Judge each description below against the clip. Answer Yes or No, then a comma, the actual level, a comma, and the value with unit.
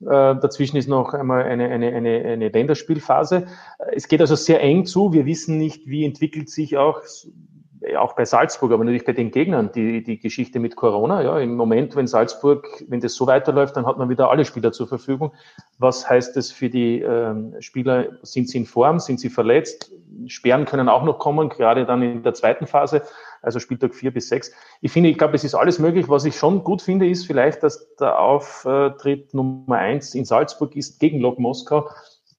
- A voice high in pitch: No, medium, 140 Hz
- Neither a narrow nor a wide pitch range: Yes, average, 3.7 semitones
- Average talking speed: No, fast, 200 wpm